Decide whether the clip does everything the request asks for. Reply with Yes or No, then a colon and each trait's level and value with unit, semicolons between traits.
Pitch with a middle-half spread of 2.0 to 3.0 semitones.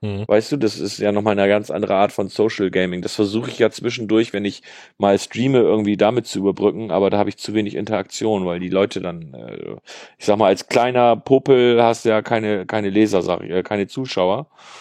Yes: average, 2.7 semitones